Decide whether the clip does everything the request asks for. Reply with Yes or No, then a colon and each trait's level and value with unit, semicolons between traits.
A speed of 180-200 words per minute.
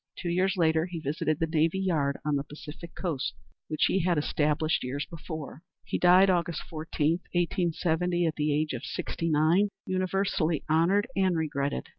No: average, 165 wpm